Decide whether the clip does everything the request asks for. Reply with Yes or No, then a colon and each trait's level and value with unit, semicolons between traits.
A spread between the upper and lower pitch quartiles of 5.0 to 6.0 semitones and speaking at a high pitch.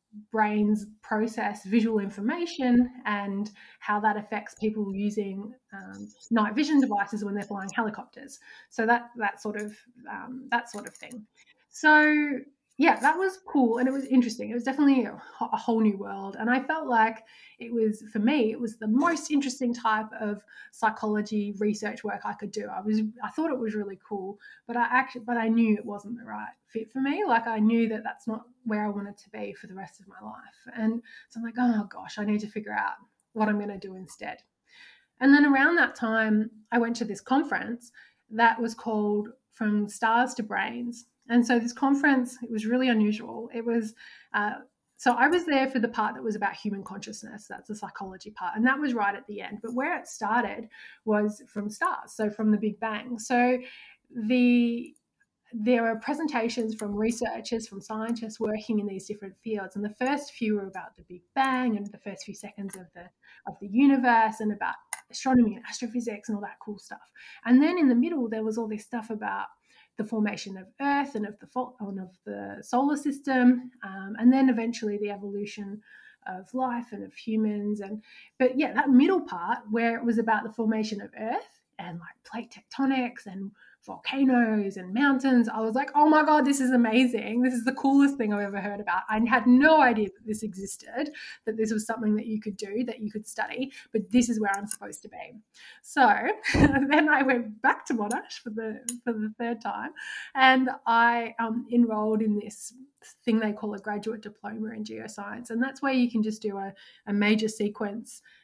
No: average, 3.1 semitones; high, 225 Hz